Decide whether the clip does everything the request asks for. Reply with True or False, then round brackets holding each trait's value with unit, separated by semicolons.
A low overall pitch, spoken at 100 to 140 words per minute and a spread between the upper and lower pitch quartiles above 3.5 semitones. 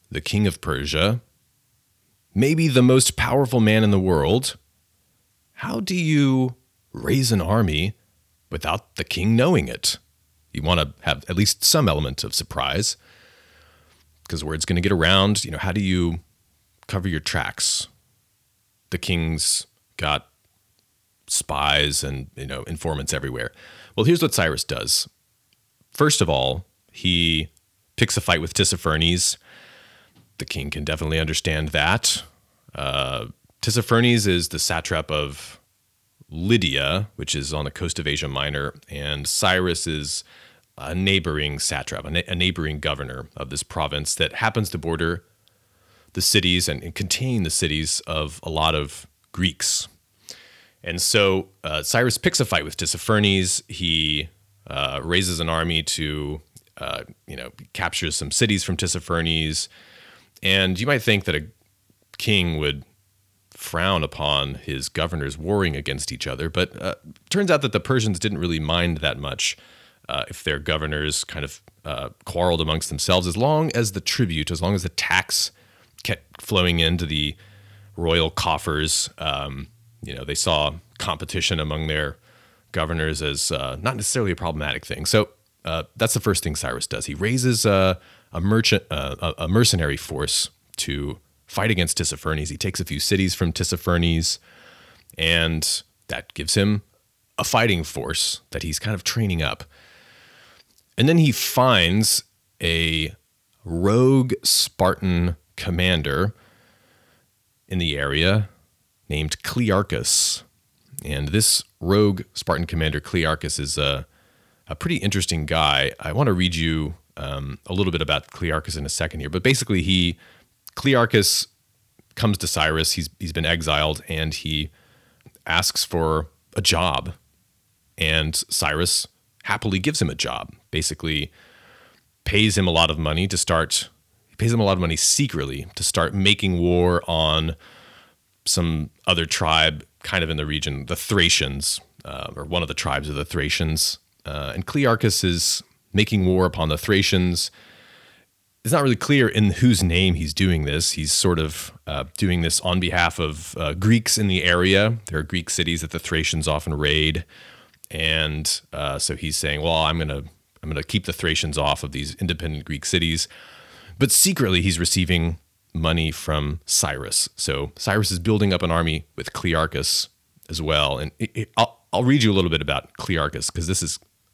False (85 Hz; 155 wpm; 4.6 semitones)